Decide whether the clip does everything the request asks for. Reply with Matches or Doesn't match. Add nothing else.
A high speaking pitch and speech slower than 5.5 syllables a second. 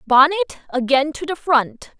Matches